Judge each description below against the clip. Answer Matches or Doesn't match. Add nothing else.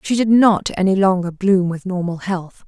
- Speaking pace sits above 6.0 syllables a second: Doesn't match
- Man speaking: Doesn't match